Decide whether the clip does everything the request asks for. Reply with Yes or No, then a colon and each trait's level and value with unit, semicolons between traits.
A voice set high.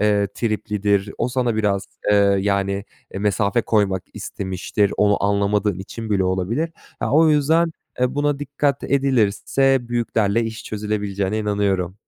No: low, 105 Hz